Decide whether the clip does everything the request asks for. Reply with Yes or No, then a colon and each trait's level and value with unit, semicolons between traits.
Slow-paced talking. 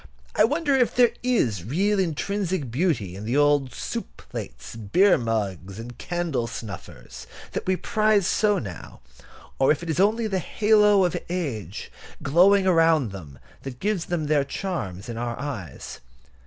No: average, 155 wpm